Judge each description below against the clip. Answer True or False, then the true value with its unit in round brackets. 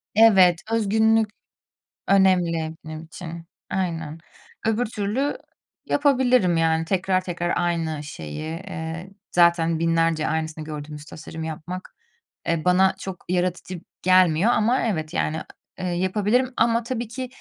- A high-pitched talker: False (180 Hz)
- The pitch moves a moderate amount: True (4.3 semitones)